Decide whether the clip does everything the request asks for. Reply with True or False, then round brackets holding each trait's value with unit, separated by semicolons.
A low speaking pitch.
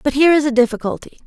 False (270 Hz)